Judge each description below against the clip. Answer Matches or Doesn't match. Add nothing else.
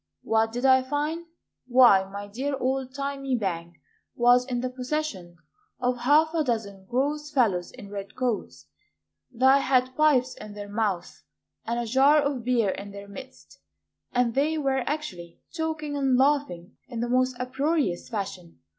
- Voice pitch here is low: Doesn't match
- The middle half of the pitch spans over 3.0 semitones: Matches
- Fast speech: Doesn't match